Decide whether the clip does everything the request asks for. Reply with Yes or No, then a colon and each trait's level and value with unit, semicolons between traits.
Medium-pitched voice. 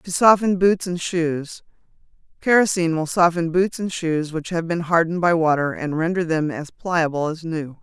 Yes: medium, 170 Hz